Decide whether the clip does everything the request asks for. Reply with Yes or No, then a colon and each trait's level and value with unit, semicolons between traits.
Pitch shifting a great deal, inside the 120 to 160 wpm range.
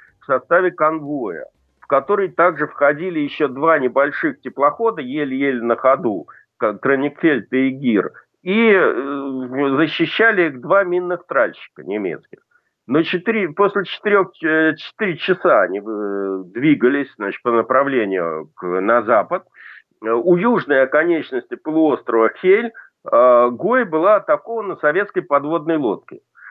No: wide, 6.6 semitones; slow, 110 wpm